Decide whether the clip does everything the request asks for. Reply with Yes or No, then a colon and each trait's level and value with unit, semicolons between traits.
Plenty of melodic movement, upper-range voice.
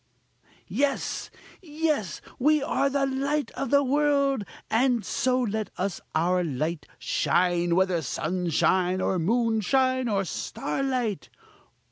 Yes: wide, 7.2 semitones; high, 225 Hz